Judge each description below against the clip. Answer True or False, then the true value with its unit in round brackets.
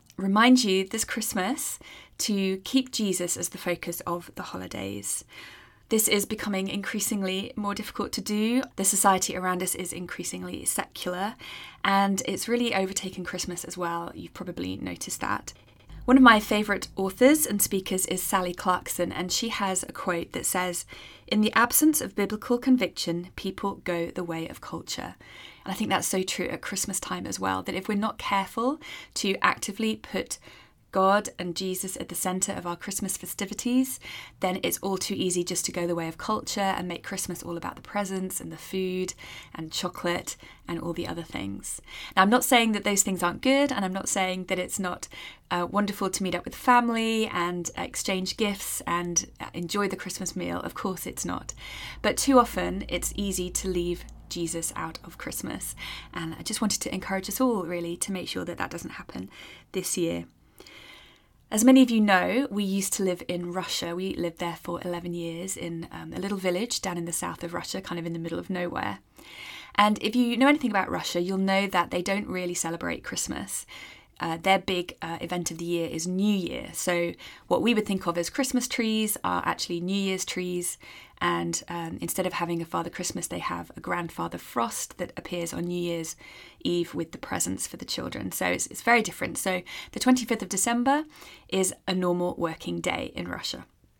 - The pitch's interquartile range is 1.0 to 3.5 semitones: True (3.2 semitones)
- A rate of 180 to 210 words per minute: True (195 wpm)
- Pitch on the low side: False (185 Hz)